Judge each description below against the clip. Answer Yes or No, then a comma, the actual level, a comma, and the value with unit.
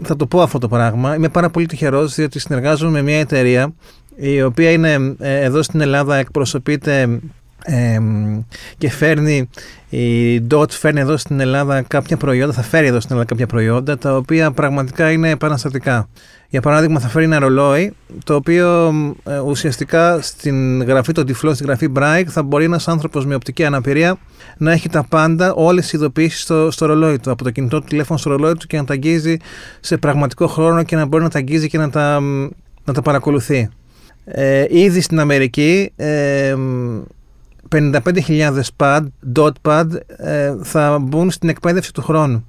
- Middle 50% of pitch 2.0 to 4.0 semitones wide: Yes, average, 2.8 semitones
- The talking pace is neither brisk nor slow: No, fast, 175 wpm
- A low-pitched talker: No, medium, 150 Hz